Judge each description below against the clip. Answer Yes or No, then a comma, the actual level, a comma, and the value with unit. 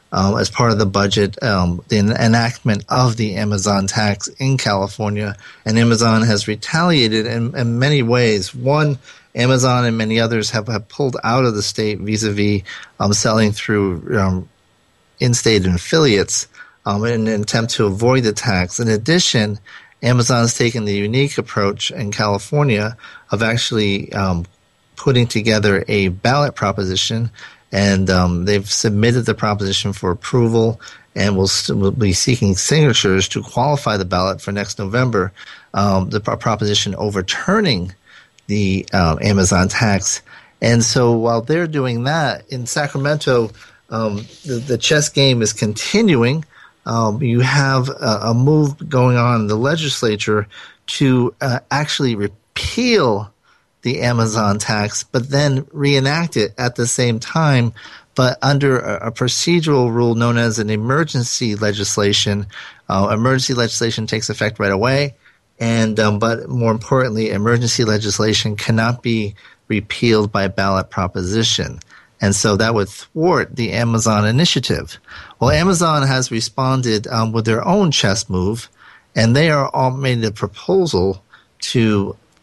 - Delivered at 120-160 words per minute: Yes, average, 145 wpm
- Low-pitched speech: Yes, low, 115 Hz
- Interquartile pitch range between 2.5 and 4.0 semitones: Yes, average, 3.5 semitones